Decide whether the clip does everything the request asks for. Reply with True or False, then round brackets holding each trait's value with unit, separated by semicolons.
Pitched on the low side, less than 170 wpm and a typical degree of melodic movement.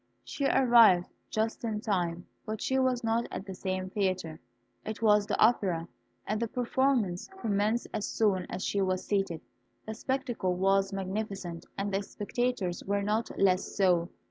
False (200 Hz; 160 wpm; 3.3 semitones)